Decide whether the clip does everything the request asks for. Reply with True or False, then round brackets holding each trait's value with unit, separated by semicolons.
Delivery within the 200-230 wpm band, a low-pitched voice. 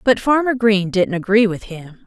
False (205 wpm; 210 Hz)